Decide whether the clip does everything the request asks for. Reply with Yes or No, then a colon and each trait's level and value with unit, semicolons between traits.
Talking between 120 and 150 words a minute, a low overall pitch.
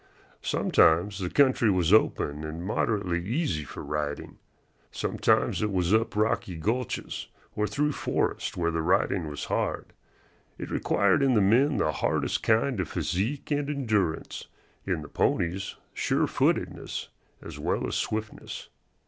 Yes: average, 140 wpm; low, 100 Hz